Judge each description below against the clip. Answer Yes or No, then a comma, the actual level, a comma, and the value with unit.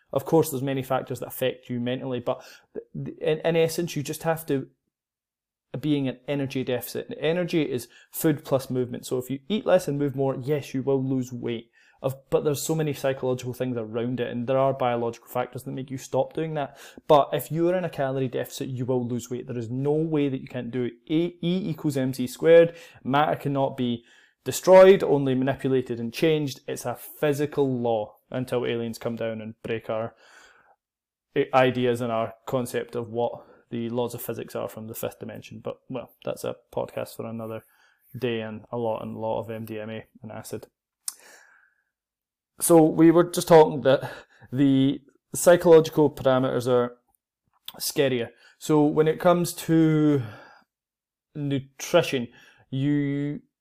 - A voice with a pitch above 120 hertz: Yes, low, 135 Hz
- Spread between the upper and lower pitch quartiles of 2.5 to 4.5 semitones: Yes, average, 3.7 semitones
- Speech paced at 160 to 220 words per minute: Yes, average, 175 wpm